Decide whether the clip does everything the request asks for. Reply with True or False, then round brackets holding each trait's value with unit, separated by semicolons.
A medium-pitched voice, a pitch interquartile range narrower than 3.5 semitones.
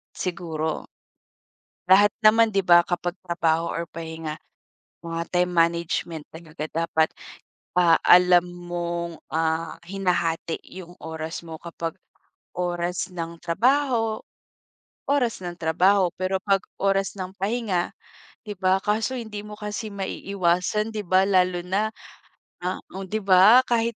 True (180 Hz; 2.9 semitones)